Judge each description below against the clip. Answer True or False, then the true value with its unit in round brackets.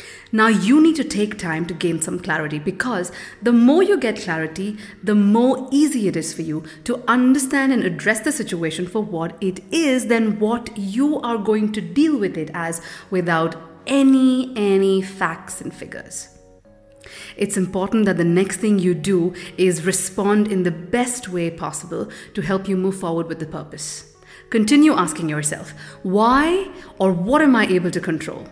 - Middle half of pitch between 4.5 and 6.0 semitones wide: True (5.5 semitones)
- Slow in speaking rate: False (175 wpm)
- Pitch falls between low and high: False (195 Hz)